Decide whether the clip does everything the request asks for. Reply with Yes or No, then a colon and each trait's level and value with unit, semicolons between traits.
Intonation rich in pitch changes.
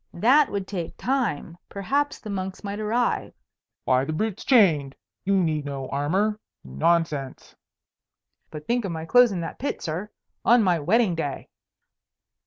Yes: wide, 6.0 semitones